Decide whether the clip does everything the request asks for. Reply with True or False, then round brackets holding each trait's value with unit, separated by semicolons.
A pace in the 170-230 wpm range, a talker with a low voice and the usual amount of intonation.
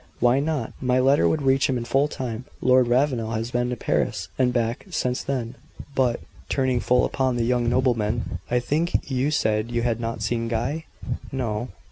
False (190 wpm; 125 Hz; 2.1 semitones)